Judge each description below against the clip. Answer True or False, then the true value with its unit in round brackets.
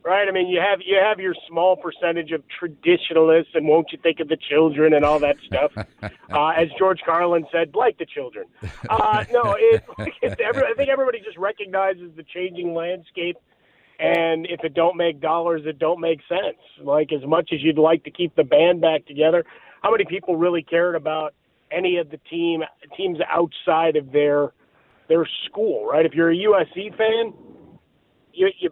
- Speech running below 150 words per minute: False (190 wpm)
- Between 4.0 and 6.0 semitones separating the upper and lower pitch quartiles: False (2.8 semitones)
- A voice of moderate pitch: True (170 Hz)